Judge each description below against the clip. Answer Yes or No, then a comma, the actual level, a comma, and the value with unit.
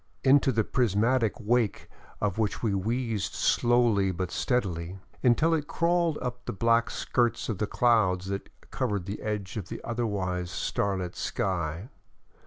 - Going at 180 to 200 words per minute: No, average, 150 wpm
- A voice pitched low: Yes, low, 110 Hz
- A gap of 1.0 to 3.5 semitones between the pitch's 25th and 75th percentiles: No, average, 4.1 semitones